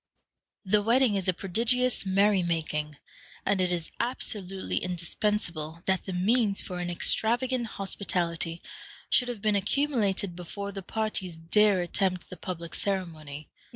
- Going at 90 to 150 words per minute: Yes, slow, 135 wpm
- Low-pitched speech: No, high, 190 Hz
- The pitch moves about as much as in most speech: Yes, average, 3.4 semitones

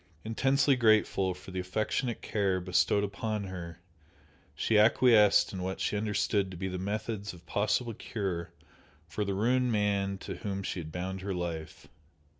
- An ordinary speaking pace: Yes, average, 160 wpm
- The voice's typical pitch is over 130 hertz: No, low, 100 Hz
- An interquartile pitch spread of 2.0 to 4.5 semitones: Yes, average, 2.8 semitones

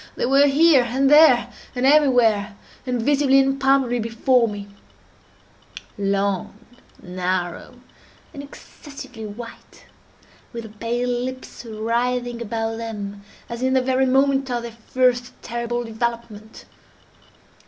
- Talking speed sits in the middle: No, slow, 120 wpm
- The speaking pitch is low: No, high, 240 Hz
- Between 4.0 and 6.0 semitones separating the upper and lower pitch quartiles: No, average, 2.9 semitones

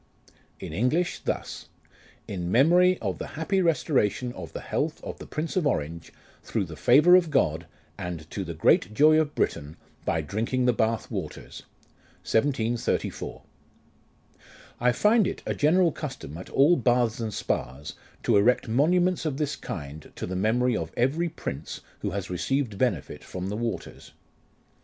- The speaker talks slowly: No, average, 160 wpm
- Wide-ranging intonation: Yes, wide, 8.6 semitones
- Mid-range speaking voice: No, low, 120 Hz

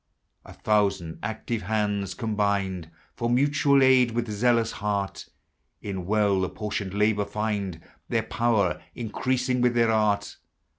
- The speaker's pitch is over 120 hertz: No, low, 105 Hz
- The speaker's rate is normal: No, slow, 120 wpm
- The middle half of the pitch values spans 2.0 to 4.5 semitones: Yes, average, 2.8 semitones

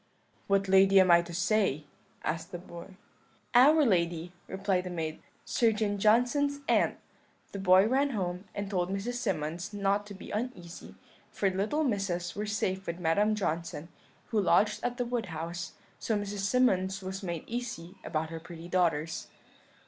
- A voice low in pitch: No, high, 195 Hz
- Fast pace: No, average, 165 wpm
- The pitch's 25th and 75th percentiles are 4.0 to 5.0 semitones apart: No, average, 3.6 semitones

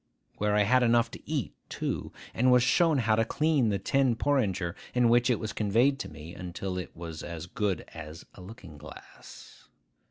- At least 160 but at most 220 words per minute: Yes, average, 190 wpm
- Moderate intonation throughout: No, wide, 5.9 semitones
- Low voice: Yes, low, 110 Hz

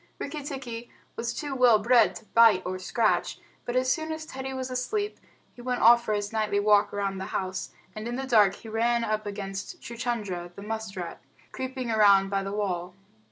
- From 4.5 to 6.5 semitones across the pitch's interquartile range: No, average, 3.9 semitones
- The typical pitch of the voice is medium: No, high, 225 Hz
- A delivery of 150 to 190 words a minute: No, average, 200 wpm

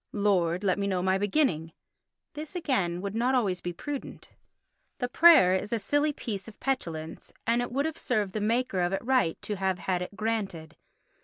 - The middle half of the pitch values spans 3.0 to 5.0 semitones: No, wide, 5.6 semitones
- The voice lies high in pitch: Yes, high, 205 Hz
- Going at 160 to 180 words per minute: No, average, 190 wpm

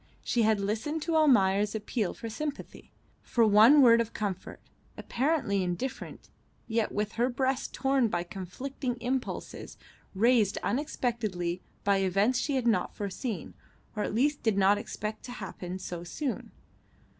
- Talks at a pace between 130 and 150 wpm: Yes, average, 145 wpm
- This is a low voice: No, high, 220 Hz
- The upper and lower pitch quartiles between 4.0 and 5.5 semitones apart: Yes, average, 4.5 semitones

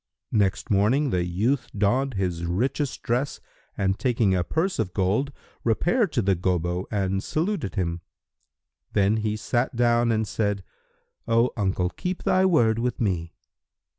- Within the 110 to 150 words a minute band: Yes, average, 145 wpm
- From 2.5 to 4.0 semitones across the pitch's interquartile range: No, average, 5.0 semitones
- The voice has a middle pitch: No, low, 110 Hz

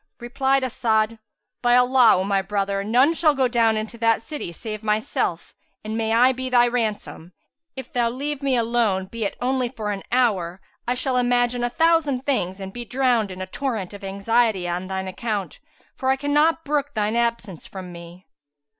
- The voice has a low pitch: No, high, 235 Hz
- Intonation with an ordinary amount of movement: Yes, average, 4.2 semitones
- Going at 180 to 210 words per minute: Yes, average, 185 wpm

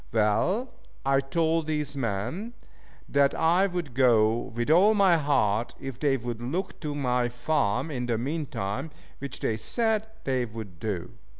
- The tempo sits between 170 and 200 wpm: No, average, 160 wpm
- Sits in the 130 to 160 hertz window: Yes, low, 135 Hz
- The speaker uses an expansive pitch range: Yes, wide, 5.8 semitones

